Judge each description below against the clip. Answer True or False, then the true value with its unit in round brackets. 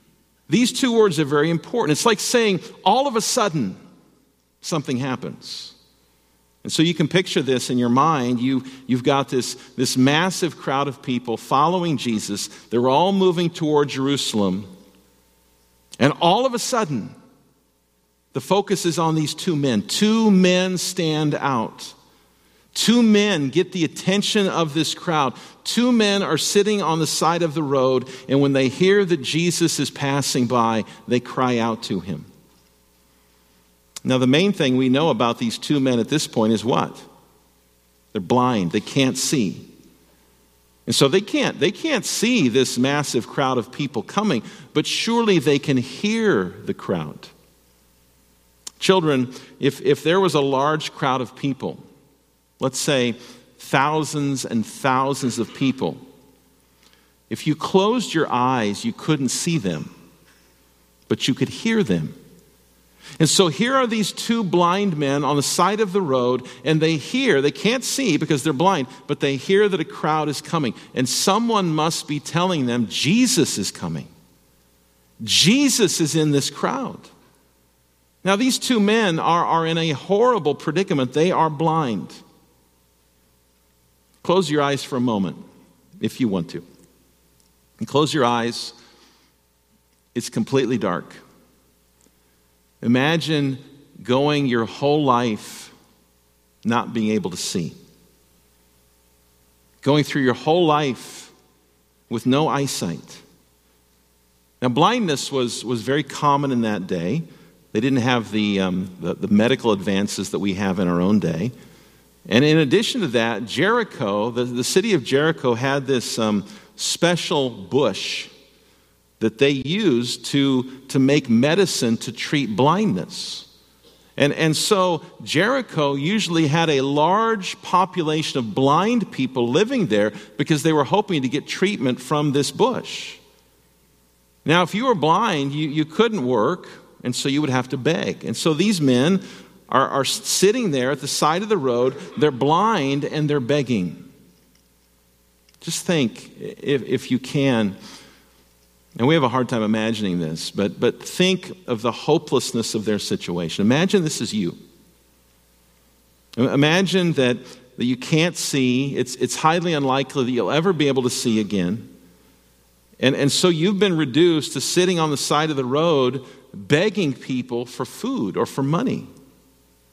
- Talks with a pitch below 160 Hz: True (140 Hz)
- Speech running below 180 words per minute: True (150 wpm)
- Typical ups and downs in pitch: False (7.2 semitones)